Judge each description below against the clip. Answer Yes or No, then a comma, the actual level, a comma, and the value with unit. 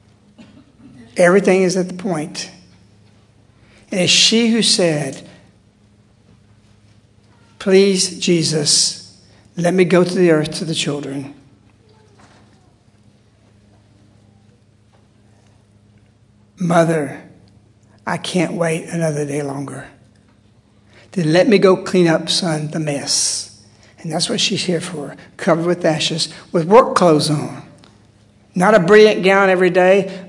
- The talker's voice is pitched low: No, medium, 145 Hz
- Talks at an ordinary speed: No, slow, 110 wpm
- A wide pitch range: Yes, wide, 8.9 semitones